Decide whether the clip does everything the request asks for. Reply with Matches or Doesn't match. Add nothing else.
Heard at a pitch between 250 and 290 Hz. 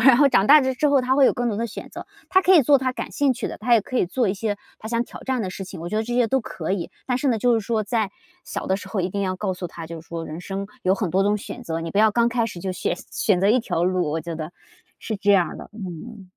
Doesn't match